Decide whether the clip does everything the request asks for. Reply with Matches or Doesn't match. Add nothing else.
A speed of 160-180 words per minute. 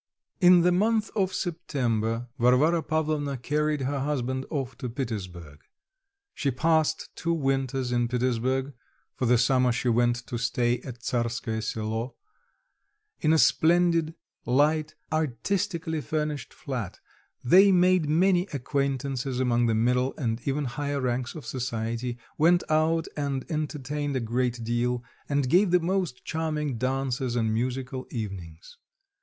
Doesn't match